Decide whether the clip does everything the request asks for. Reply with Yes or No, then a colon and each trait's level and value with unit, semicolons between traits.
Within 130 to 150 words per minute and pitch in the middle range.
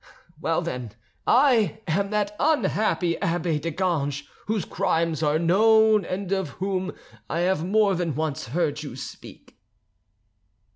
Yes: slow, 135 wpm; medium, 180 Hz